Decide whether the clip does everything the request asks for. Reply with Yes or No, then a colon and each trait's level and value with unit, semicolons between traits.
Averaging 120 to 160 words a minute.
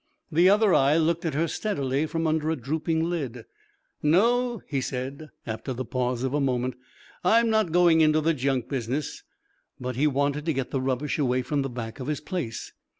No: average, 195 wpm